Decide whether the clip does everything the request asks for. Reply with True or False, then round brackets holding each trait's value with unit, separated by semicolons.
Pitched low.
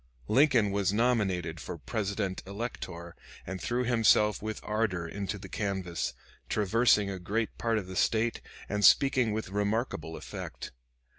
True (105 Hz)